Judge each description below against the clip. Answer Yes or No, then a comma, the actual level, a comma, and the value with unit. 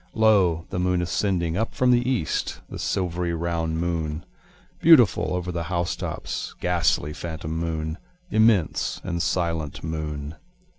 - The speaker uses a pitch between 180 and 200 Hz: No, very low, 85 Hz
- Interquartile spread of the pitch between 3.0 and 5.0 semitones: No, narrow, 2.5 semitones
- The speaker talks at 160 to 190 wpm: No, slow, 135 wpm